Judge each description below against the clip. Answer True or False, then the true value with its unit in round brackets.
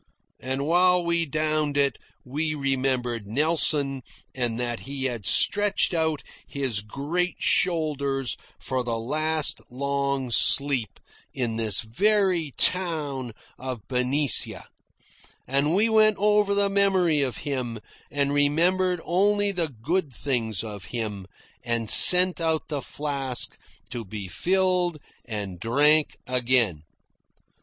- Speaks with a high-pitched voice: False (140 Hz)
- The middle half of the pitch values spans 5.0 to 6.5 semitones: True (5.5 semitones)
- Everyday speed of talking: False (120 wpm)